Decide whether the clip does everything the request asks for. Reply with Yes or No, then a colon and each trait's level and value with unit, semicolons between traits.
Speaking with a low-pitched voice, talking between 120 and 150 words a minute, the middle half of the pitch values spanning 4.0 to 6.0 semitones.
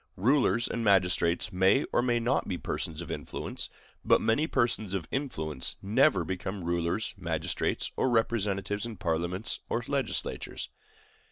Yes: low, 100 Hz; average, 140 wpm; average, 5.1 semitones